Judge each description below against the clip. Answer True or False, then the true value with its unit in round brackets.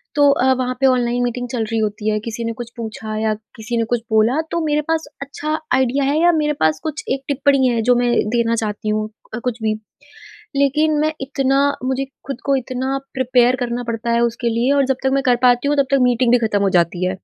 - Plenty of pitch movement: False (3.1 semitones)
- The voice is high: True (245 Hz)